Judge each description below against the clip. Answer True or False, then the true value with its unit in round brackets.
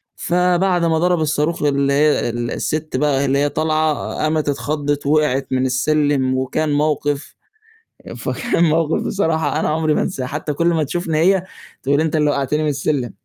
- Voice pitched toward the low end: False (150 Hz)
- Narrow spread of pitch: True (2.2 semitones)